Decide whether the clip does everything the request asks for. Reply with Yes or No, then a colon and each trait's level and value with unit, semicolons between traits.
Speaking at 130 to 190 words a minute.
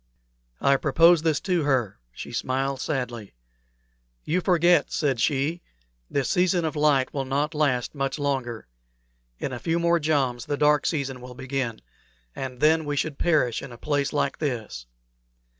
Yes: average, 160 wpm